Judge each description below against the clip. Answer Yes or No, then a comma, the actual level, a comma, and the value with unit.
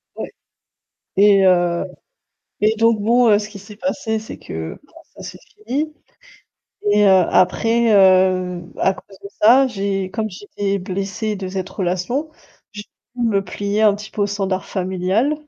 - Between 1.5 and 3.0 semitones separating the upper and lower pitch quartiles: Yes, average, 2.7 semitones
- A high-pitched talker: Yes, high, 200 Hz